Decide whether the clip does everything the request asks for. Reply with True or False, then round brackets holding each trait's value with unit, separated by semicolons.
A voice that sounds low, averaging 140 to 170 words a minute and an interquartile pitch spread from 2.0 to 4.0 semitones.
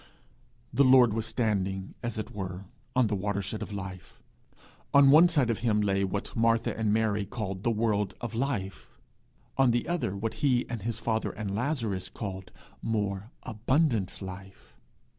True (110 Hz; 160 wpm; 3.2 semitones)